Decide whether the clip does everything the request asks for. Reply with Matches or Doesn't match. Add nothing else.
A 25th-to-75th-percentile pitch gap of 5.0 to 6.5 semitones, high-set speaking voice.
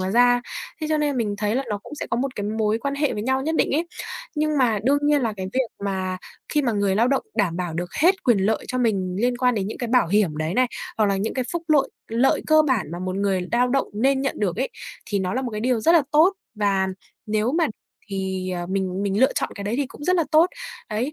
Matches